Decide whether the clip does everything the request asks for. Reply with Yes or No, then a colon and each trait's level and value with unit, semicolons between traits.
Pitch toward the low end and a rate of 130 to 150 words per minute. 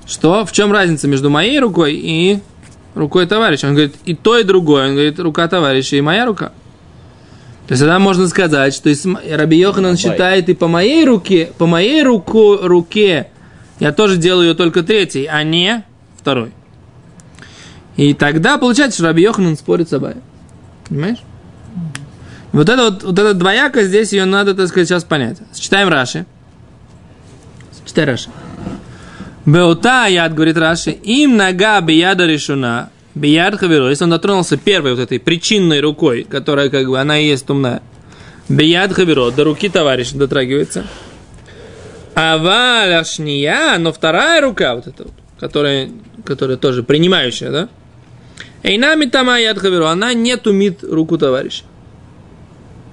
No: medium, 170 Hz; average, 145 wpm